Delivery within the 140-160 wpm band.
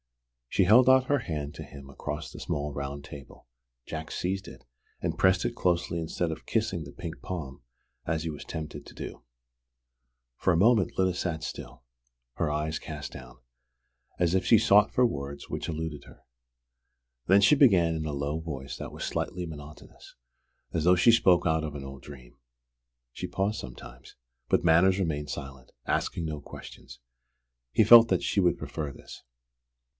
No: average, 175 wpm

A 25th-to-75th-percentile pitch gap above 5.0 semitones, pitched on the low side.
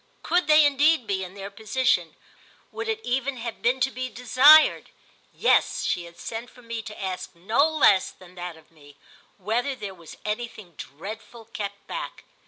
No: wide, 5.6 semitones; high, 225 Hz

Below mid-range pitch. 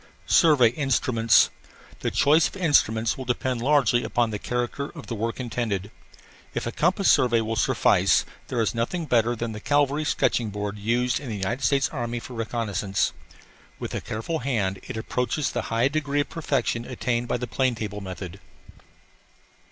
Yes: low, 120 Hz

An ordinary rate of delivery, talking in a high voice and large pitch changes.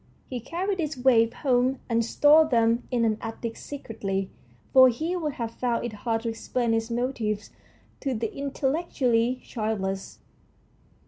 No: average, 150 wpm; high, 240 Hz; average, 3.0 semitones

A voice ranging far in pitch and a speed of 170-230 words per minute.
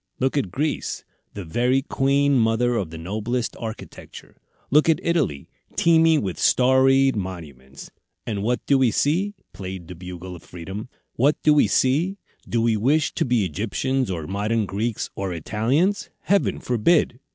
No: wide, 6.3 semitones; average, 155 wpm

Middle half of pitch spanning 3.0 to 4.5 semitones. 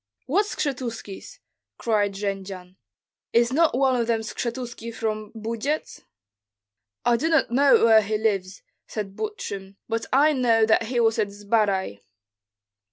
Yes: average, 3.6 semitones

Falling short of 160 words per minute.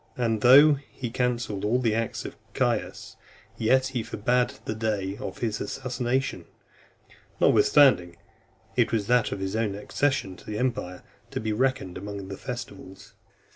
Yes: average, 150 wpm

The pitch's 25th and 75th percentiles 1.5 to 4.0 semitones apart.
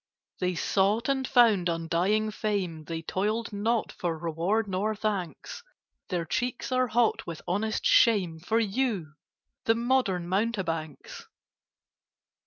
No: average, 4.8 semitones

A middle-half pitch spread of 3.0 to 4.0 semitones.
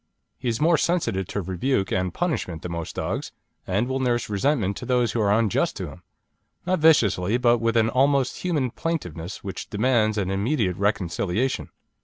No: average, 5.3 semitones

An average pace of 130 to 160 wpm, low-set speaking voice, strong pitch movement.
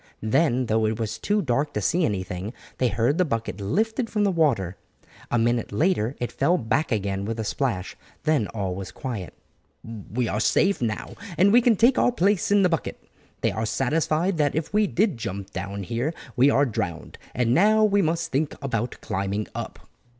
No: average, 190 wpm; low, 125 Hz; wide, 7.8 semitones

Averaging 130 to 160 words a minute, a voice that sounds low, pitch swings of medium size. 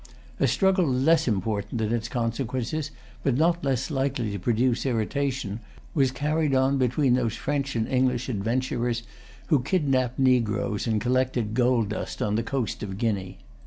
Yes: average, 155 wpm; low, 125 Hz; average, 3.2 semitones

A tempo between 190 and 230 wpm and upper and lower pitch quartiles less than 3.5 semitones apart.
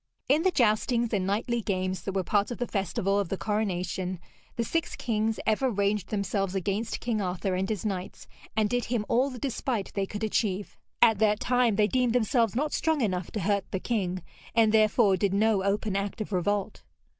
Yes: average, 200 wpm; average, 3.1 semitones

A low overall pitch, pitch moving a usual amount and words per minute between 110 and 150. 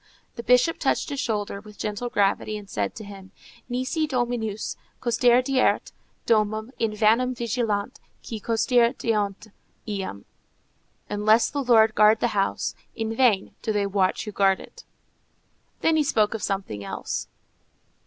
No: high, 220 Hz; average, 3.0 semitones; average, 140 wpm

